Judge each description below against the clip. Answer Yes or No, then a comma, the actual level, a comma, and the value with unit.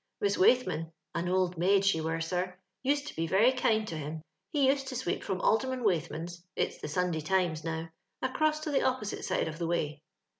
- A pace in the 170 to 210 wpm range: Yes, average, 200 wpm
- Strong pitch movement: Yes, wide, 7.5 semitones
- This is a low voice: No, medium, 185 Hz